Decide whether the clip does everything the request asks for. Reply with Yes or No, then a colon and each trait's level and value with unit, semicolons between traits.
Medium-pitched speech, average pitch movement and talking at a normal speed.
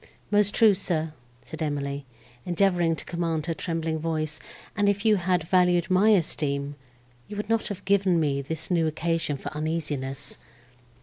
Yes: medium, 165 Hz; average, 3.4 semitones; average, 160 wpm